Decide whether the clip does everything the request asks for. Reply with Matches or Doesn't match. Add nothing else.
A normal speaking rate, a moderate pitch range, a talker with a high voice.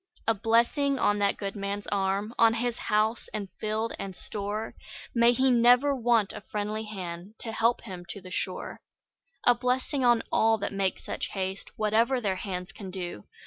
Matches